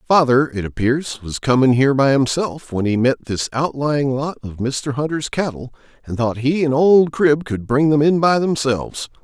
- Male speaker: Yes, male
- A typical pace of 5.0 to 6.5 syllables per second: No, 4.7 syllables/s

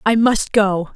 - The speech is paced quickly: No, average, 190 wpm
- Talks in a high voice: Yes, high, 210 Hz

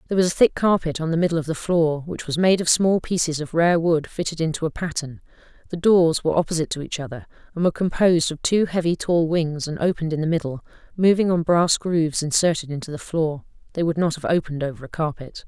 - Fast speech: Yes, fast, 230 wpm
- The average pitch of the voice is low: No, medium, 165 Hz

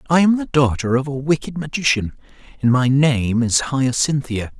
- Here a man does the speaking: Yes, male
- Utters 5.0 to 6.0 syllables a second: No, 4.8 syllables/s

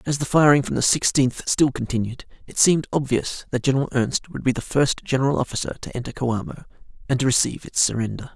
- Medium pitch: No, low, 130 Hz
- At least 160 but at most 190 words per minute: No, average, 200 wpm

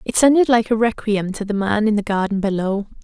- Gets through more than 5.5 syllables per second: Yes, 5.8 syllables/s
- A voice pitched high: Yes, high, 210 Hz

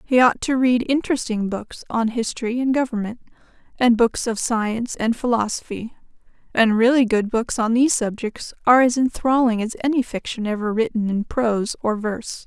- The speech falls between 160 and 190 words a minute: Yes, average, 170 wpm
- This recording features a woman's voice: Yes, female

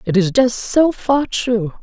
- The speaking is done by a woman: Yes, female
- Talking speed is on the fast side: No, average, 195 wpm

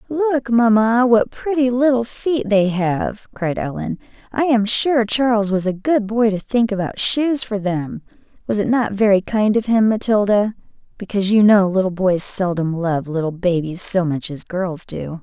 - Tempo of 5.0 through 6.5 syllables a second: No, 4.5 syllables/s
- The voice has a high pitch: Yes, high, 210 Hz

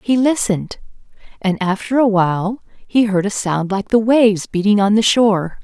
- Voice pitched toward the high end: Yes, high, 210 Hz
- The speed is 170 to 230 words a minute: Yes, average, 180 wpm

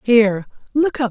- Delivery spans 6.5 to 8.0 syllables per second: No, 4.9 syllables/s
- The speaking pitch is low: No, high, 235 Hz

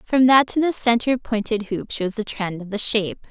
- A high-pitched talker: Yes, high, 225 Hz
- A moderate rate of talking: No, fast, 235 wpm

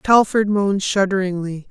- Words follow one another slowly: Yes, slow, 105 wpm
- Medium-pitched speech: No, high, 195 Hz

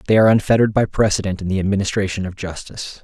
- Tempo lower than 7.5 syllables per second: No, 7.7 syllables/s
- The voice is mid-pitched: No, low, 100 Hz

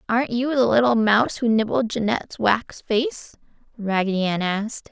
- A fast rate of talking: No, average, 160 wpm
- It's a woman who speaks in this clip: Yes, female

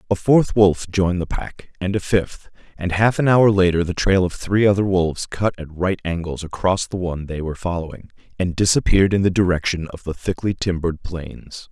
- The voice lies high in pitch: No, very low, 90 Hz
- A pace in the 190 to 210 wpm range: Yes, fast, 205 wpm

